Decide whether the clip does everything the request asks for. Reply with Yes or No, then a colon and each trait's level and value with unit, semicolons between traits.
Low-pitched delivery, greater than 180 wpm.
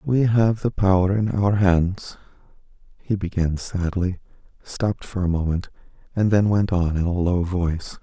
No: very low, 95 Hz; average, 165 wpm